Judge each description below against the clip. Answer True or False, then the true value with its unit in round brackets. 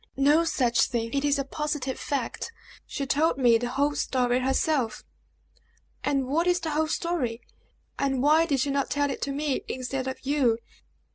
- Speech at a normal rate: True (180 wpm)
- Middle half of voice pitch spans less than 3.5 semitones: True (2.6 semitones)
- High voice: True (275 Hz)